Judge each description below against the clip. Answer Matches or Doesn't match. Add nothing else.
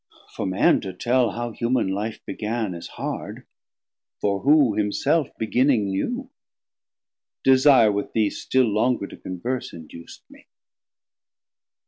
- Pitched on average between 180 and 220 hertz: Doesn't match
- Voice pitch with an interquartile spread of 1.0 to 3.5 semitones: Doesn't match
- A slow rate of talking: Matches